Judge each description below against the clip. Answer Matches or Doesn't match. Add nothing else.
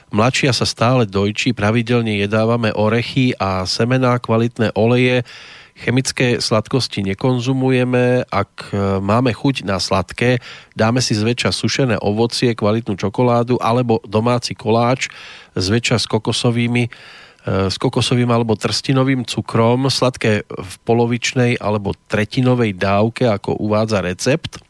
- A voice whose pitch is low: Matches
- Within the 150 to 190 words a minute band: Doesn't match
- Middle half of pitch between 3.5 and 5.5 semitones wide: Doesn't match